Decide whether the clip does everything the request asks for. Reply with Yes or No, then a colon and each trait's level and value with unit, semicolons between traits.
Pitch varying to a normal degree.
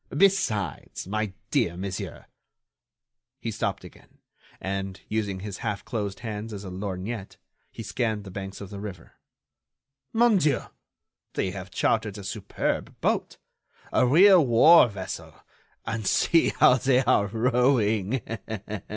Yes: average, 4.2 semitones